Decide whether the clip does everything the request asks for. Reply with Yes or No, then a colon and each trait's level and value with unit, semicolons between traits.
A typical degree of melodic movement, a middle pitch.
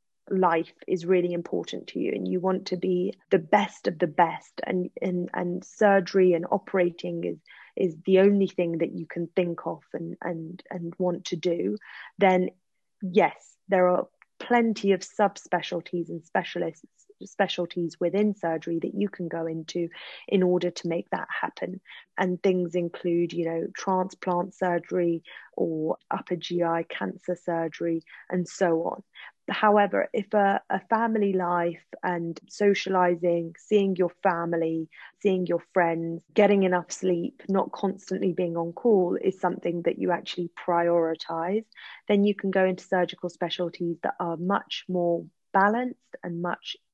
No: narrow, 1.9 semitones; medium, 180 Hz